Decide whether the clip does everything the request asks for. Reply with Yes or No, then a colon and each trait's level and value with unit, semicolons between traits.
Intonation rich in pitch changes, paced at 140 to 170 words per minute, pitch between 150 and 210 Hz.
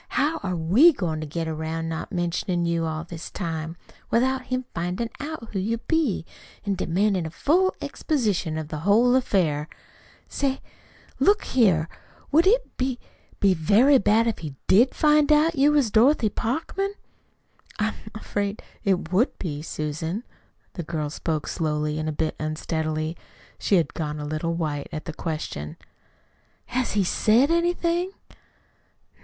Yes: wide, 8.2 semitones; average, 150 wpm; high, 190 Hz